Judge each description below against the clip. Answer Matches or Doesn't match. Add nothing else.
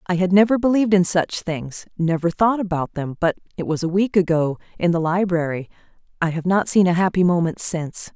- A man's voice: Doesn't match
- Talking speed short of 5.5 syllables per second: Doesn't match